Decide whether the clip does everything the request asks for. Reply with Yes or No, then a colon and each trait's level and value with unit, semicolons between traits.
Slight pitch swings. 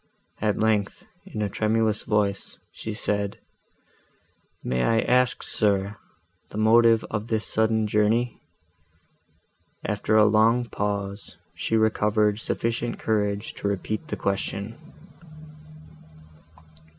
Yes: narrow, 1.5 semitones